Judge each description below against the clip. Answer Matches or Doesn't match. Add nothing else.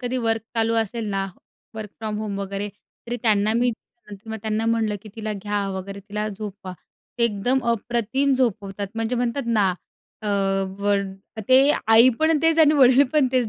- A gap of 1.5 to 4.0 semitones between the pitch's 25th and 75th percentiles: Matches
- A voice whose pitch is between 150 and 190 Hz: Doesn't match